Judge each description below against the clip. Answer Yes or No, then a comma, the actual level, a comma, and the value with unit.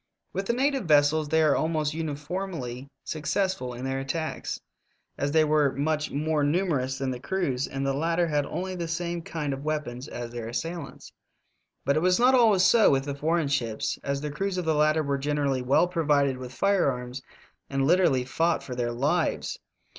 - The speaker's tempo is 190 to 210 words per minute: Yes, average, 195 wpm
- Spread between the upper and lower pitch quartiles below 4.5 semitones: Yes, average, 3.8 semitones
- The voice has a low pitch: No, medium, 150 Hz